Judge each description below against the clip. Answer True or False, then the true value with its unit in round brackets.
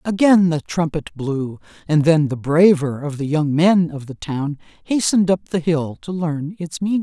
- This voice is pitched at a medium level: True (160 Hz)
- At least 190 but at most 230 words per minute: True (195 wpm)